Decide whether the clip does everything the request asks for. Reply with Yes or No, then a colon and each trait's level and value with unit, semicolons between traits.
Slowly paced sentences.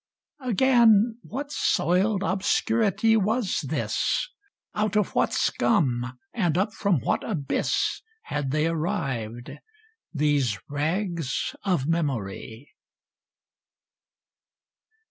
Yes: slow, 95 wpm